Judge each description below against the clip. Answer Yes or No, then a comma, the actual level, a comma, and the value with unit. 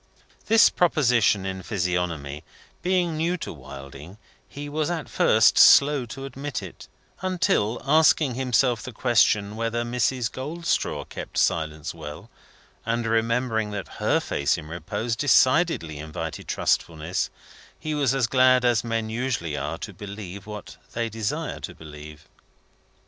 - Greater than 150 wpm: No, slow, 135 wpm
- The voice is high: No, low, 115 Hz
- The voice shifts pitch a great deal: Yes, wide, 7.2 semitones